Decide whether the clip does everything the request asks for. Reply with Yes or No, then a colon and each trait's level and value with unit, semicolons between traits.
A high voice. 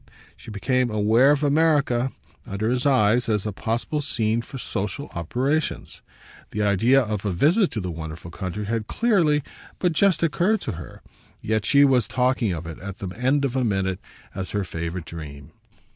No: low, 115 Hz